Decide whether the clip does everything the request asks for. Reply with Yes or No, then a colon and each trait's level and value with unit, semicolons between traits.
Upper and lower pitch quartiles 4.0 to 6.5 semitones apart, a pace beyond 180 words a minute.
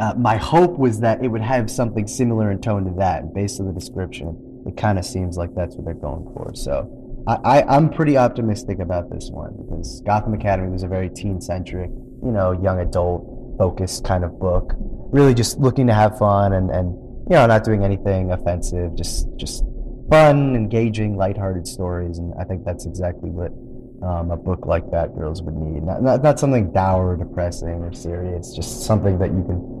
Yes: average, 5.0 semitones; average, 200 wpm